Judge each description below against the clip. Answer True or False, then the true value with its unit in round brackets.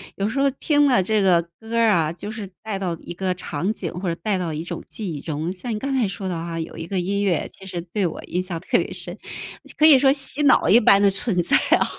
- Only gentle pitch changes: False (4.3 semitones)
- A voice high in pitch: True (195 Hz)